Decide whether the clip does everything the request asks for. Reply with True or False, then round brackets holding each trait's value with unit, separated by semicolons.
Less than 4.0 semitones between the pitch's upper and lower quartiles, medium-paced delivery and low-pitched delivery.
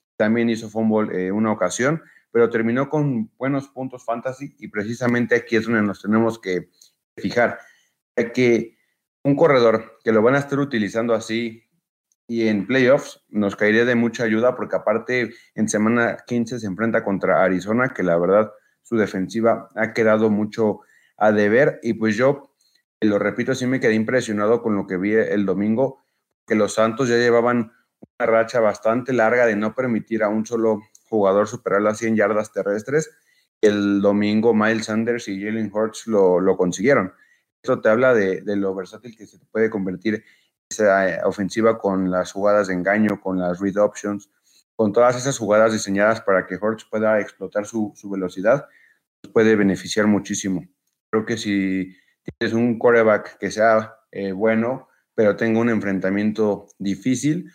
True (2.4 semitones; 165 wpm; 110 Hz)